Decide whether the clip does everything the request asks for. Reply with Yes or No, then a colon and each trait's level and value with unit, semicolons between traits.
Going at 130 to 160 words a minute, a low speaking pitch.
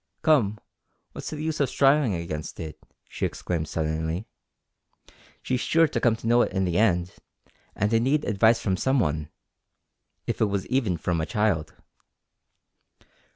Yes: average, 155 wpm; low, 105 Hz